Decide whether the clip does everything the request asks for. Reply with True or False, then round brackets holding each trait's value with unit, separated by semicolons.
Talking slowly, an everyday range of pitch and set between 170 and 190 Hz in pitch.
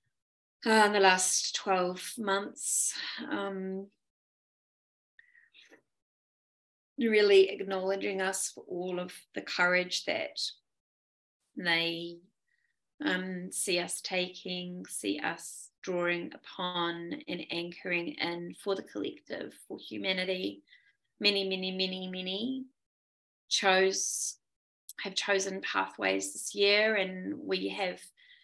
False (95 wpm; 2.2 semitones; 185 Hz)